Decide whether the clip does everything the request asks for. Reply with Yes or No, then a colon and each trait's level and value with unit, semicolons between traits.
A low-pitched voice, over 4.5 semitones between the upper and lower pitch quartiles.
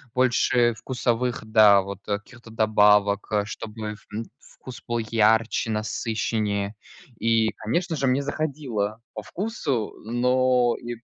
No: low, 115 Hz; average, 2.8 semitones